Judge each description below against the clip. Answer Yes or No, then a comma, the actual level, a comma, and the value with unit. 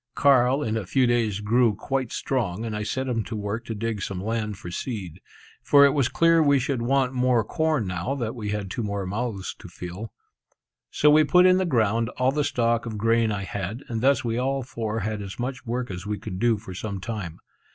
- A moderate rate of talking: No, fast, 225 wpm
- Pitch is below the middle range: Yes, low, 115 Hz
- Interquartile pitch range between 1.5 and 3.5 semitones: No, average, 4.0 semitones